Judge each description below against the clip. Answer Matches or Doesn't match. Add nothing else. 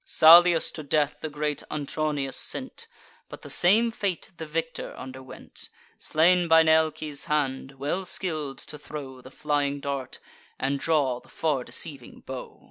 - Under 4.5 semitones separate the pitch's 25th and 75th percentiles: Matches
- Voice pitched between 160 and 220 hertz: Doesn't match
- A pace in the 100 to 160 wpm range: Matches